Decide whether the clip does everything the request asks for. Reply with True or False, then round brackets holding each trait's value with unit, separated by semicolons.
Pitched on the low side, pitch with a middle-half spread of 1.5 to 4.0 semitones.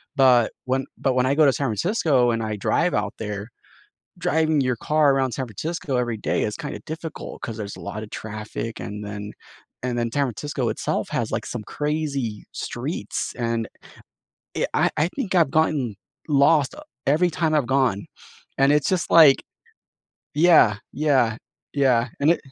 False (130 Hz; 5.0 semitones)